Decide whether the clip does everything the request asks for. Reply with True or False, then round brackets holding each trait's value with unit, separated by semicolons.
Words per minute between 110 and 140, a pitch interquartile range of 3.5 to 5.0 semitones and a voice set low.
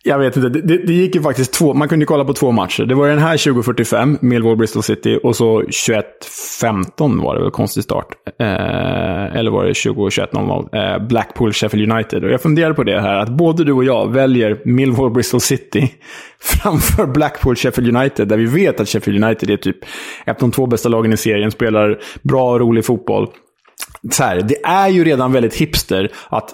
False (195 wpm; 4.0 semitones; 125 Hz)